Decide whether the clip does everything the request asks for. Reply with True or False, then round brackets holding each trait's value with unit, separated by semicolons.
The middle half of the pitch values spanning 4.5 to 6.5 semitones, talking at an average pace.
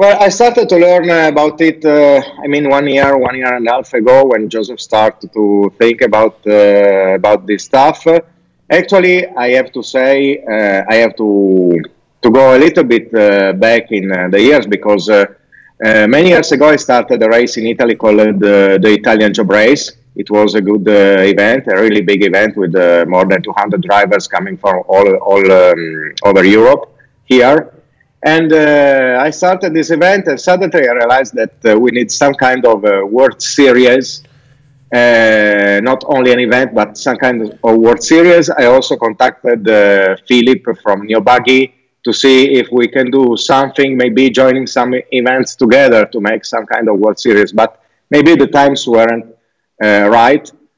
True (4.9 semitones; 180 wpm)